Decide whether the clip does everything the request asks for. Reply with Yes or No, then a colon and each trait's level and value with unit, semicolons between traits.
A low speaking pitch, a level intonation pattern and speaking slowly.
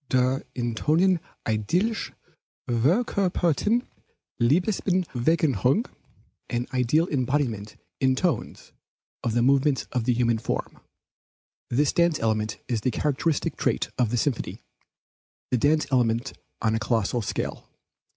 No: low, 130 Hz; wide, 5.4 semitones; slow, 115 wpm